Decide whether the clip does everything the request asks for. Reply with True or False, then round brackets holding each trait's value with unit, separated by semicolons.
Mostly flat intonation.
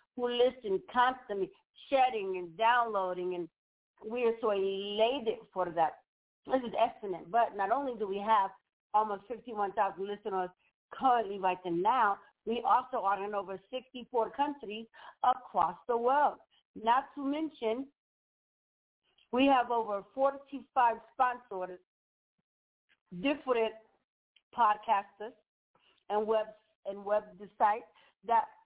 False (4.1 semitones)